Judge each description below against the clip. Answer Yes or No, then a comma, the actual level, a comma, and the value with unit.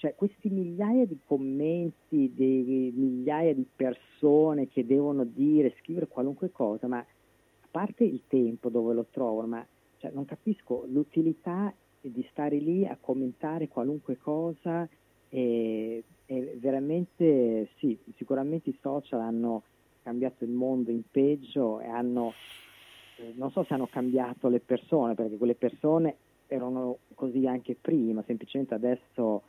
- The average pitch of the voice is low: Yes, low, 130 Hz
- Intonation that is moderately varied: Yes, average, 4.0 semitones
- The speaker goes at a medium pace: Yes, average, 135 wpm